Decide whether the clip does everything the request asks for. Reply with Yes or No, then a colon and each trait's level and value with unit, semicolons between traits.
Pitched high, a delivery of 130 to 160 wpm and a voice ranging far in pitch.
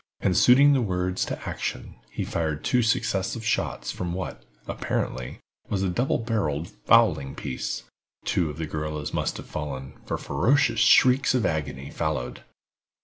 No: very low, 90 Hz; average, 150 wpm; wide, 7.5 semitones